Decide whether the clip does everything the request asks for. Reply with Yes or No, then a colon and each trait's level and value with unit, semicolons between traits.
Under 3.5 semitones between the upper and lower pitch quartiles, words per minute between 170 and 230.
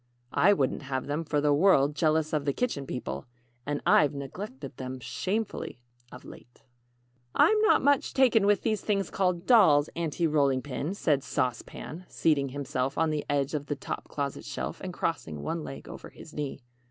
No: average, 4.8 semitones; average, 180 wpm